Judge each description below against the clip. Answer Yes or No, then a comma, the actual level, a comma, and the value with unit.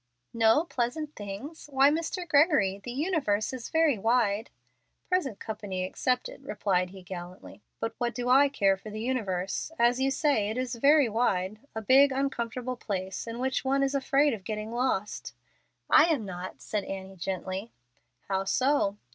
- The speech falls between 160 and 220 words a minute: Yes, average, 165 wpm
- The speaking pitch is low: No, high, 235 Hz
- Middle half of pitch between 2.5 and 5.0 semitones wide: No, wide, 5.5 semitones